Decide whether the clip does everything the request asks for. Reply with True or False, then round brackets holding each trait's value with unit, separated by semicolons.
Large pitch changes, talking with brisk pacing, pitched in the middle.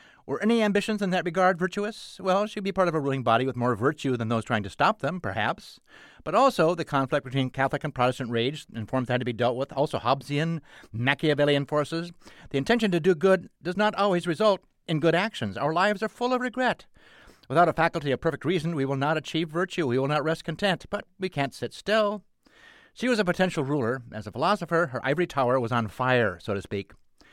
True (6.2 semitones; 225 wpm; 160 Hz)